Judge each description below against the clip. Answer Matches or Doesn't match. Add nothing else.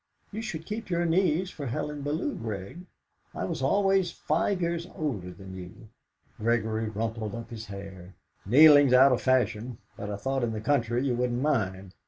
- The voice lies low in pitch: Matches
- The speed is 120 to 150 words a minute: Doesn't match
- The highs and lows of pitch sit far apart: Matches